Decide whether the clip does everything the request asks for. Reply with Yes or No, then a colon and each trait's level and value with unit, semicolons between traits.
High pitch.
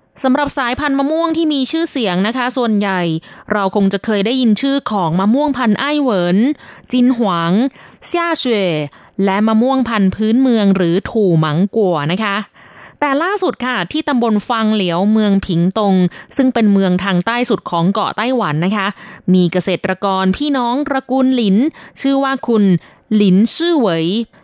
Yes: high, 215 Hz